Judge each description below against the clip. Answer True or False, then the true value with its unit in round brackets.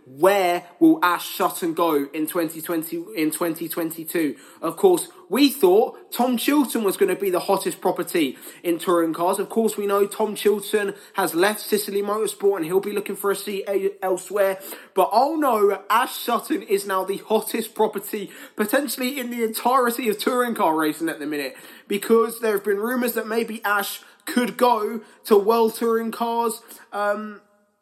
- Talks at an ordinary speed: True (170 wpm)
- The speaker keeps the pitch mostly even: False (3.7 semitones)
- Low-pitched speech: False (205 Hz)